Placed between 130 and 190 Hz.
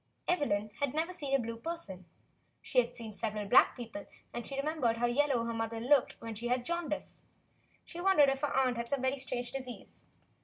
No: very high, 250 Hz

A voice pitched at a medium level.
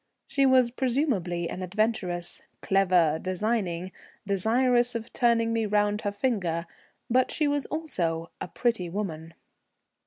No: high, 210 Hz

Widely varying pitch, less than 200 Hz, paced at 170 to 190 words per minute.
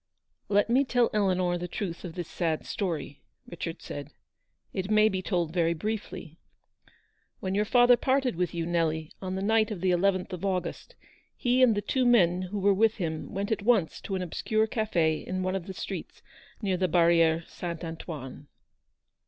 No: average, 3.9 semitones; medium, 185 Hz; average, 185 wpm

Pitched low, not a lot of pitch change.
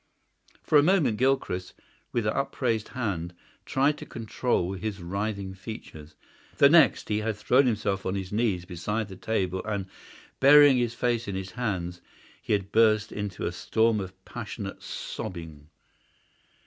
No: low, 105 Hz; average, 4.0 semitones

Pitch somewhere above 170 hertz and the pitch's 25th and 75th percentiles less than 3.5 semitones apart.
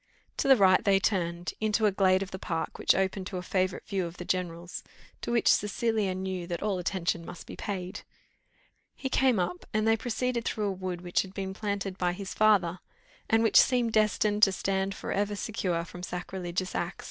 Yes: high, 190 Hz; average, 2.8 semitones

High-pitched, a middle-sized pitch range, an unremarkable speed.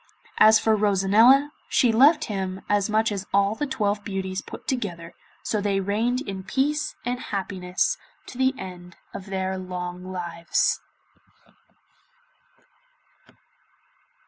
No: high, 200 Hz; average, 3.8 semitones; slow, 120 wpm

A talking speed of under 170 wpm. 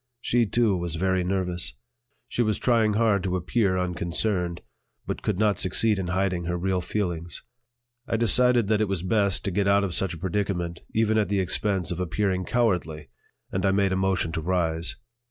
No: average, 190 wpm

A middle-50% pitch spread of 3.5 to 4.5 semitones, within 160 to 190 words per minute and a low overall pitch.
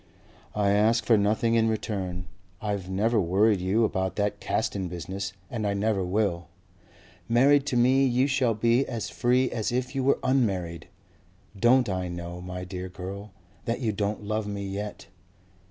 Yes: average, 3.8 semitones; average, 165 wpm; low, 105 Hz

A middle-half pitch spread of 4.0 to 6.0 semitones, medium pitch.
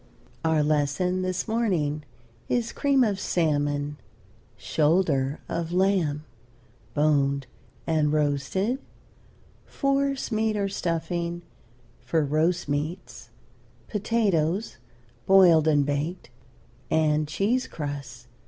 Yes: average, 4.7 semitones; medium, 160 Hz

